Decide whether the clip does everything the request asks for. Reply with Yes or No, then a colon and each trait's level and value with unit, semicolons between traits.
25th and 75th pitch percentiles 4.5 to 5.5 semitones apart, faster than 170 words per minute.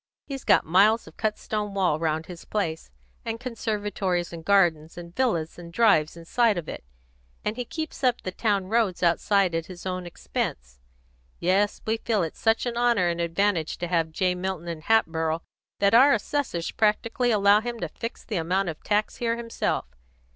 Yes: average, 4.9 semitones; average, 185 wpm